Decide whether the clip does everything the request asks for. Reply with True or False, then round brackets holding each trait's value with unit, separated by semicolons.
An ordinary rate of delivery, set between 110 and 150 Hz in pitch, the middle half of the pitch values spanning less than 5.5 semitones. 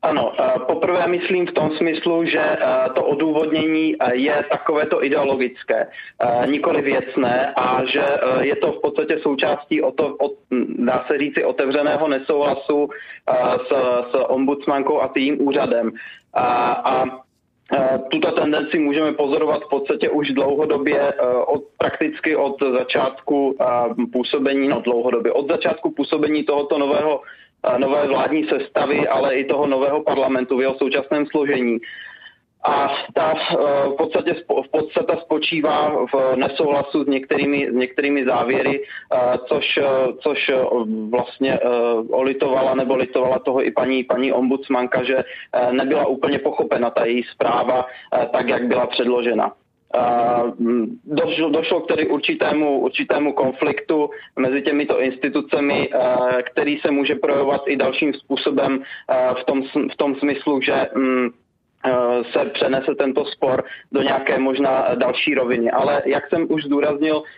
True (130 wpm; 140 Hz; 2.7 semitones)